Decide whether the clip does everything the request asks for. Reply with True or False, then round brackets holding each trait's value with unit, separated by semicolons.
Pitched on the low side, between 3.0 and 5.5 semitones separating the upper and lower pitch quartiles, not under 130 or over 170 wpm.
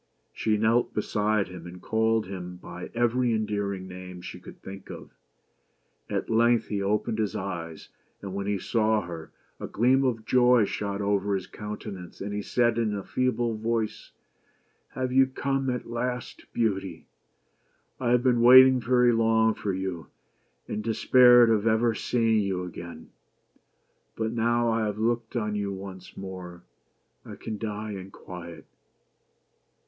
True (110 Hz; 3.3 semitones; 155 wpm)